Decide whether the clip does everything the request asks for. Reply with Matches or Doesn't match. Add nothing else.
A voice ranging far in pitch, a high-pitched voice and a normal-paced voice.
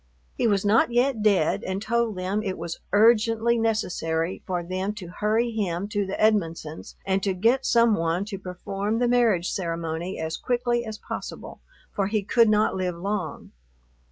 Doesn't match